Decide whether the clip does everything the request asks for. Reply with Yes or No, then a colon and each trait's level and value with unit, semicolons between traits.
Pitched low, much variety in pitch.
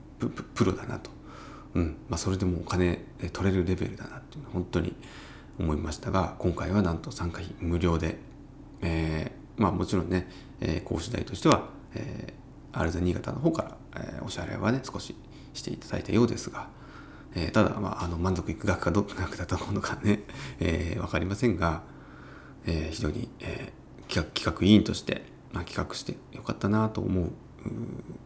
No: very low, 95 Hz; average, 4.0 semitones